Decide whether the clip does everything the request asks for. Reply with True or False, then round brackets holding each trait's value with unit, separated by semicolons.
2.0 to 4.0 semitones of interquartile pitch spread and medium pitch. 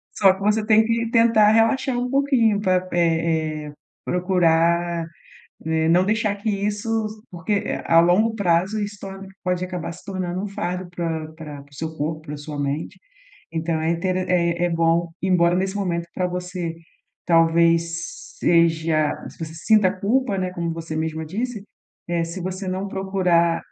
True (3.1 semitones; 180 Hz)